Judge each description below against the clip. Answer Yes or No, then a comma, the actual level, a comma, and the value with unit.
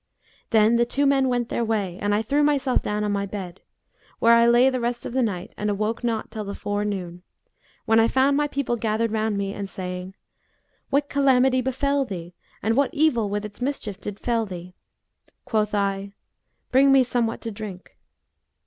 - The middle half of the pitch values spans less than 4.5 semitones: Yes, average, 4.0 semitones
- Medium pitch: No, high, 225 Hz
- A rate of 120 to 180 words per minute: No, average, 190 wpm